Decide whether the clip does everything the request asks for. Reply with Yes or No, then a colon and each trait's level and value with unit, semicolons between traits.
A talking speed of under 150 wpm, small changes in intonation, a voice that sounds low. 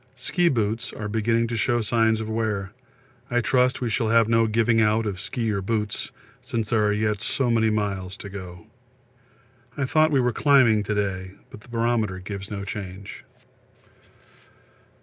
No: average, 170 wpm; narrow, 2.3 semitones; low, 110 Hz